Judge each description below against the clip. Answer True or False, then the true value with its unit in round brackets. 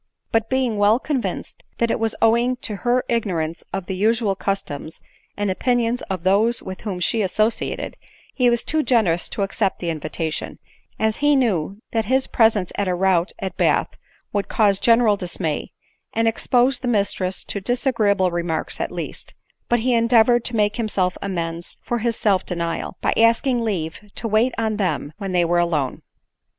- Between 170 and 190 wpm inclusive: True (175 wpm)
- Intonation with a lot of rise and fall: False (4.2 semitones)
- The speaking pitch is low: False (210 Hz)